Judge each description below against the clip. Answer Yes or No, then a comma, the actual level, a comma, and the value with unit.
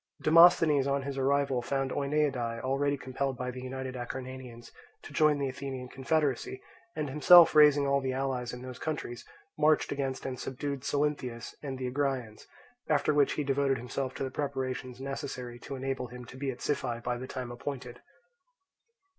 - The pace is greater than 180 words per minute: No, average, 170 wpm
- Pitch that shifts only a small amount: Yes, narrow, 1.9 semitones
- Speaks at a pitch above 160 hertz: No, low, 135 Hz